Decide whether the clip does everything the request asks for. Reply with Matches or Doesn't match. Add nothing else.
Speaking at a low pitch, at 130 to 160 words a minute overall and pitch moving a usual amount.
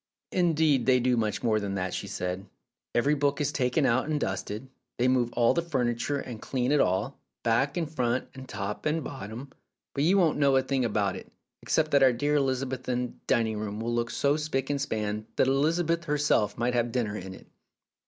Doesn't match